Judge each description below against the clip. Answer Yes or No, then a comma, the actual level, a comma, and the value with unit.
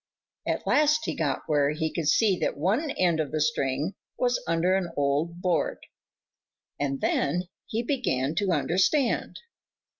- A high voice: No, medium, 170 Hz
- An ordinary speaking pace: Yes, average, 150 wpm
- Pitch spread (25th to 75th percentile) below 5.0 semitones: No, wide, 5.5 semitones